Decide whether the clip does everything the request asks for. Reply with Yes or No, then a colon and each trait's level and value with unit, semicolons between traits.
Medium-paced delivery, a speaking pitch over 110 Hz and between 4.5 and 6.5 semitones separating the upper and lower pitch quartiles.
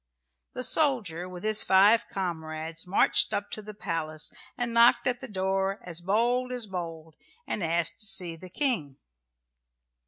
Yes: average, 155 wpm; high, 190 Hz; wide, 5.4 semitones